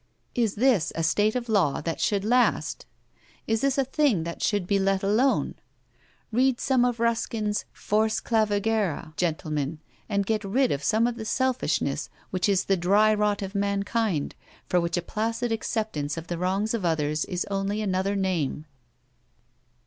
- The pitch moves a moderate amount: Yes, average, 3.8 semitones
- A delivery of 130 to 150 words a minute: No, average, 165 wpm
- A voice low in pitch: No, high, 205 Hz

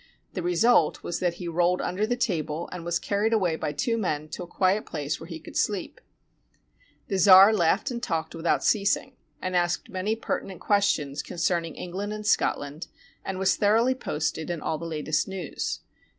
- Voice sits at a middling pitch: Yes, medium, 180 Hz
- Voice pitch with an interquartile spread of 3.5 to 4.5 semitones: Yes, average, 3.8 semitones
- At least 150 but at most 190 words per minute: Yes, average, 180 wpm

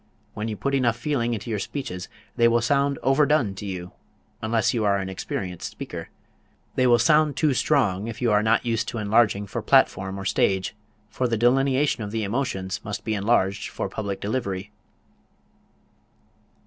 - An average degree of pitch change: Yes, average, 4.4 semitones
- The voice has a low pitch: Yes, low, 110 Hz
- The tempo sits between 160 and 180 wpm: Yes, average, 175 wpm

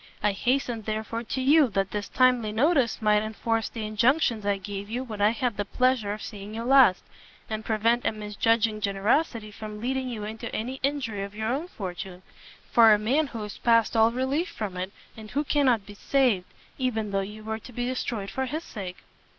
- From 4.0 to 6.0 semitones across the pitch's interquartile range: No, average, 3.4 semitones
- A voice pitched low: No, high, 220 Hz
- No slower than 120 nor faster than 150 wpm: No, average, 200 wpm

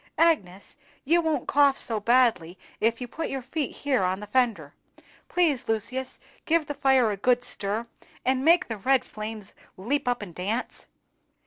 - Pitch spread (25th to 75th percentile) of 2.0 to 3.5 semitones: No, average, 4.8 semitones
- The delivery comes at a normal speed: Yes, average, 165 wpm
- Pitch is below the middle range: No, high, 245 Hz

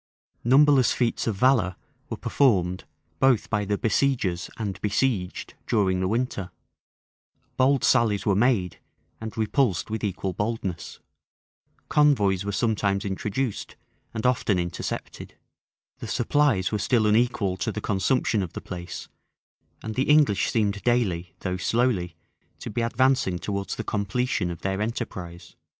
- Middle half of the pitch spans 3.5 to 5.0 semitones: Yes, average, 4.4 semitones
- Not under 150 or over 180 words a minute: No, slow, 135 wpm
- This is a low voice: Yes, low, 105 Hz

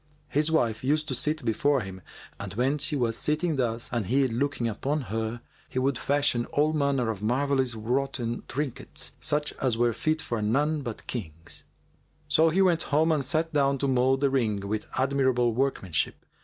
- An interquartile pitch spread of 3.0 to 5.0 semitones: Yes, average, 3.9 semitones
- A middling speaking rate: Yes, average, 185 wpm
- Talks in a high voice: No, low, 130 Hz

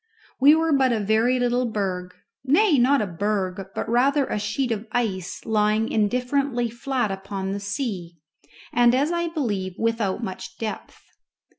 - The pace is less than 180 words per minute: Yes, average, 155 wpm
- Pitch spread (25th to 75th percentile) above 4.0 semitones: Yes, average, 4.6 semitones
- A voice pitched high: Yes, high, 225 Hz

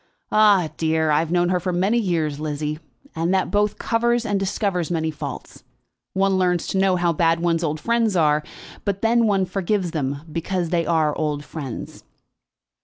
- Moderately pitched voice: Yes, medium, 175 Hz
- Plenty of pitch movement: No, average, 3.6 semitones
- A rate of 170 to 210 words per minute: Yes, average, 180 wpm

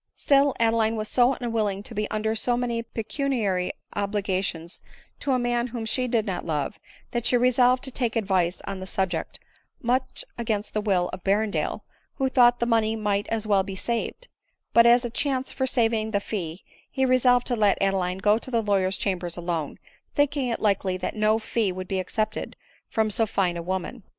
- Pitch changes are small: No, average, 3.9 semitones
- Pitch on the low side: No, high, 220 Hz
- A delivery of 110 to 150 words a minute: No, average, 195 wpm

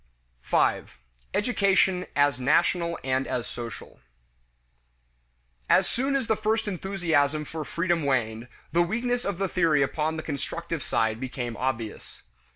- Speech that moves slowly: Yes, slow, 130 wpm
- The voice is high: No, medium, 160 Hz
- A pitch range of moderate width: No, wide, 6.4 semitones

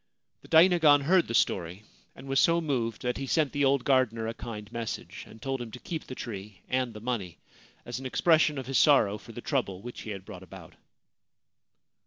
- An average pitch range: Yes, average, 4.6 semitones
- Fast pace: Yes, fast, 210 wpm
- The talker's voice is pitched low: Yes, low, 125 Hz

